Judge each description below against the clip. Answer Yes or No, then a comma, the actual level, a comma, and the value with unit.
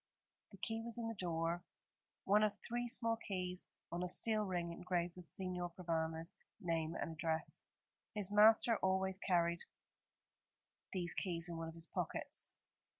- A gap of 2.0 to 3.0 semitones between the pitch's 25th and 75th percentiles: No, average, 3.6 semitones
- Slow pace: No, average, 150 wpm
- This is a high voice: No, medium, 180 Hz